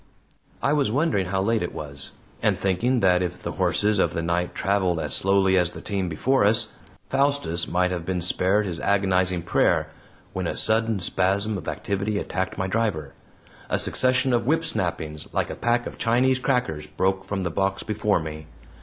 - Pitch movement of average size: Yes, average, 4.0 semitones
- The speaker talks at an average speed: Yes, average, 185 wpm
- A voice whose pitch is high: No, very low, 95 Hz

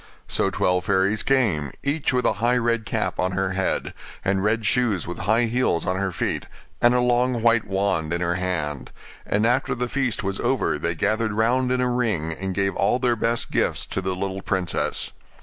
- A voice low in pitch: Yes, low, 105 Hz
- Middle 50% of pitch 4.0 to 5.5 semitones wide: Yes, average, 4.6 semitones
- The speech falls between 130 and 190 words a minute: No, average, 200 wpm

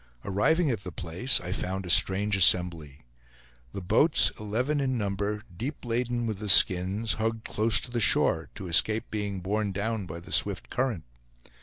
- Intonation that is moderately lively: Yes, average, 3.9 semitones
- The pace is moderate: Yes, average, 170 wpm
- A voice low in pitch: Yes, low, 105 Hz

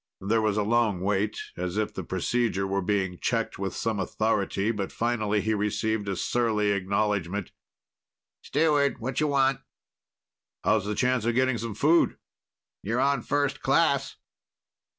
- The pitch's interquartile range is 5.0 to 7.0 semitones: No, average, 3.3 semitones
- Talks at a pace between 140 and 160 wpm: Yes, average, 145 wpm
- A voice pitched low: Yes, low, 110 Hz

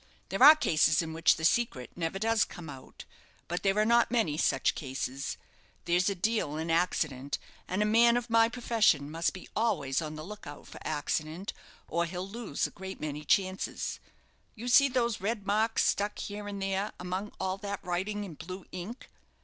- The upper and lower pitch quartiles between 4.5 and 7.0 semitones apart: Yes, average, 5.1 semitones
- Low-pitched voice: No, high, 190 Hz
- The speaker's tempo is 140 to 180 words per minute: No, average, 190 wpm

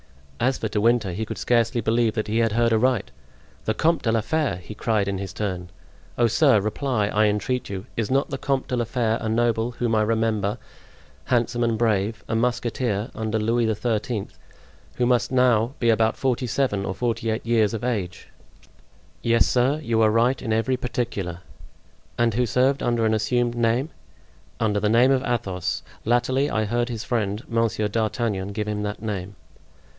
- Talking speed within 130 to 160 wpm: No, average, 185 wpm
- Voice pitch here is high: No, low, 115 Hz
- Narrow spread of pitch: Yes, narrow, 2.3 semitones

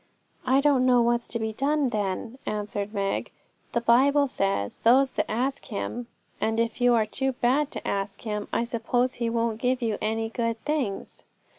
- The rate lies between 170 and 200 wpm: Yes, average, 180 wpm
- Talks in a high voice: Yes, high, 235 Hz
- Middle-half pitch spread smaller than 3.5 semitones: Yes, average, 2.9 semitones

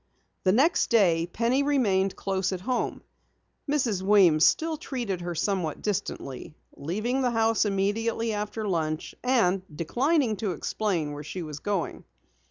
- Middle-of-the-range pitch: No, high, 205 Hz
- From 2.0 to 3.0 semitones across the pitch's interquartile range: No, average, 4.9 semitones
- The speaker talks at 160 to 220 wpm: No, average, 140 wpm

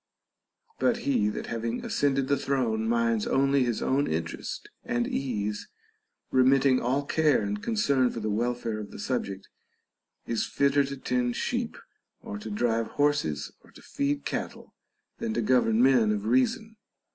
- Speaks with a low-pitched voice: Yes, low, 120 Hz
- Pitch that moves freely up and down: No, average, 3.9 semitones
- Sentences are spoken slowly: No, average, 155 wpm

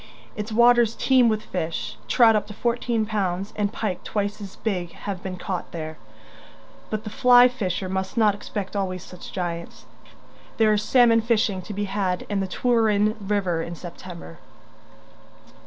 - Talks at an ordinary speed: Yes, average, 155 wpm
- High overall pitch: Yes, high, 205 Hz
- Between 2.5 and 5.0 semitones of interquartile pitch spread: Yes, average, 3.2 semitones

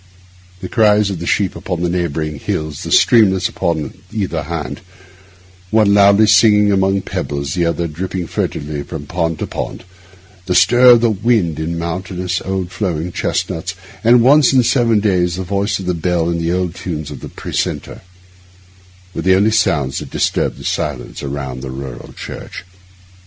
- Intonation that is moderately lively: Yes, average, 3.9 semitones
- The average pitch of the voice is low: Yes, very low, 90 Hz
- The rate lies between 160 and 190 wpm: Yes, average, 170 wpm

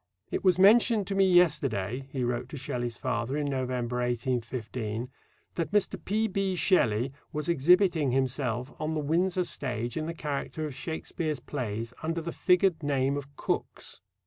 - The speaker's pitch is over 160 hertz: No, medium, 145 Hz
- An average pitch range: No, wide, 5.7 semitones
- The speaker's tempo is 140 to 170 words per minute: Yes, average, 155 wpm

